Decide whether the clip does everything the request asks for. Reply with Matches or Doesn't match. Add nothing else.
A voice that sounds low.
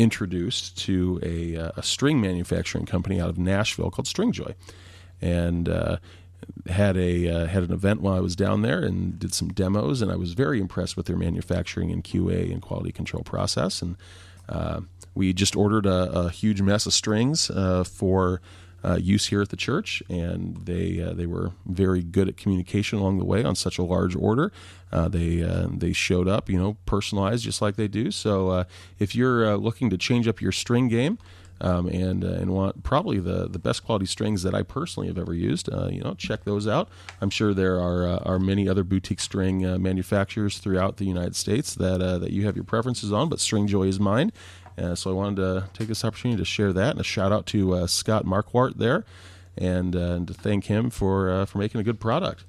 Matches